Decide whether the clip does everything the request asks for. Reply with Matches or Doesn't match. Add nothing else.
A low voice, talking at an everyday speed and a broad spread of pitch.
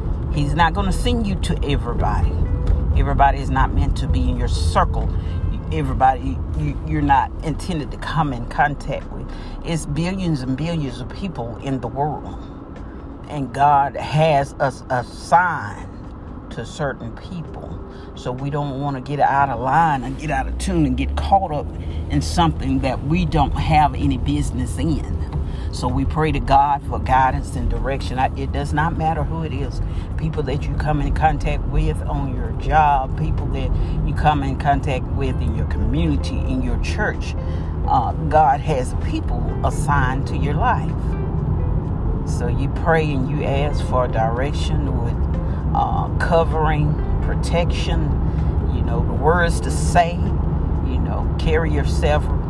Matches